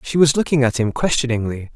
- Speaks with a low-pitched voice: Yes, low, 130 Hz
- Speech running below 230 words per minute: Yes, fast, 205 wpm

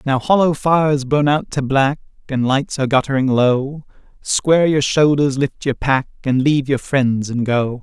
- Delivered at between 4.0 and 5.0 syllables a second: Yes, 4.6 syllables/s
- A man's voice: Yes, male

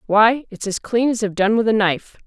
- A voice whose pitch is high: Yes, high, 215 Hz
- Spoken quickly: Yes, fast, 265 wpm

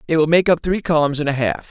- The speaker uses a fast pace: Yes, fast, 315 wpm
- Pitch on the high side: No, medium, 155 Hz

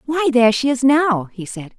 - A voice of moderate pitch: No, very high, 250 Hz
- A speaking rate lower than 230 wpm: No, fast, 235 wpm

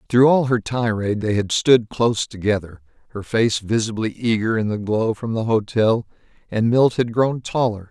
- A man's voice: Yes, male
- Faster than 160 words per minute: Yes, average, 180 wpm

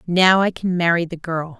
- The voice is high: No, medium, 175 Hz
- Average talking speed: No, fast, 225 wpm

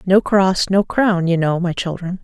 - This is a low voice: No, medium, 185 Hz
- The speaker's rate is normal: No, fast, 215 wpm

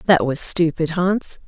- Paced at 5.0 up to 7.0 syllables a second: No, 3.9 syllables/s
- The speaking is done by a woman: Yes, female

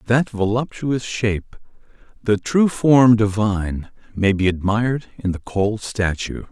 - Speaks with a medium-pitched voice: No, low, 110 Hz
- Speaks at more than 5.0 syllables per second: No, 4.1 syllables/s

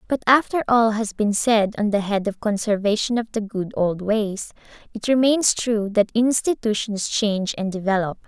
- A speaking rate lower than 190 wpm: Yes, average, 175 wpm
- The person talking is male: No, female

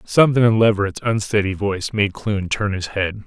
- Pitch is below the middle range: Yes, low, 105 Hz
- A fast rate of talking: No, average, 185 wpm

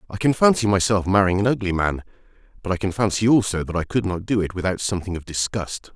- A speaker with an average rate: No, fast, 230 wpm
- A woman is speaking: No, male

